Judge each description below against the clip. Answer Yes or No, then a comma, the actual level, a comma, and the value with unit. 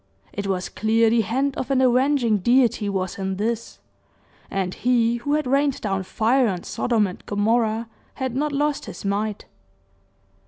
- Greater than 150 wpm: Yes, average, 160 wpm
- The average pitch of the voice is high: Yes, high, 230 Hz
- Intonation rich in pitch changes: No, average, 4.3 semitones